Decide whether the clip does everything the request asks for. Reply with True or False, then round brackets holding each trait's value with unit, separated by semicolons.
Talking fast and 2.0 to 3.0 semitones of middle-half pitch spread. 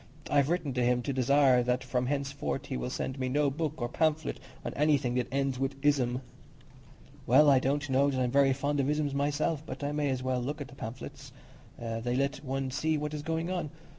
True (220 wpm; 2.4 semitones)